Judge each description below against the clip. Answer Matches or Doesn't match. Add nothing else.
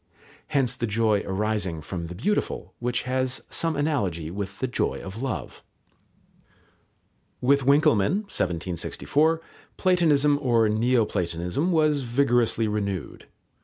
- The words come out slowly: Matches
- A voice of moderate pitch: Doesn't match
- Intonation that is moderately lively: Doesn't match